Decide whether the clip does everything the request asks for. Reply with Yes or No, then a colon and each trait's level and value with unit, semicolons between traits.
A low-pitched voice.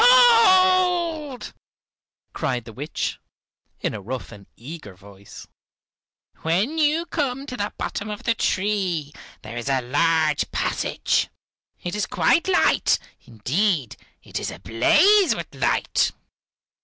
No: high, 190 Hz